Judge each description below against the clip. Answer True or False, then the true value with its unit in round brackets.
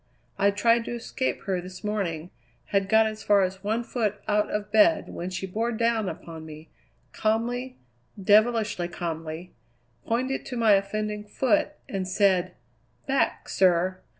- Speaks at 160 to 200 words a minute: False (150 wpm)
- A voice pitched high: True (205 Hz)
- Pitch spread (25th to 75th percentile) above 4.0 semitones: False (3.4 semitones)